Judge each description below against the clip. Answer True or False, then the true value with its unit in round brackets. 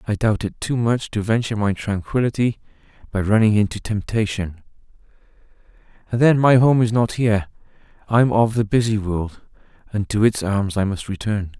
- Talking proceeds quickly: False (165 wpm)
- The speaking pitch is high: False (105 Hz)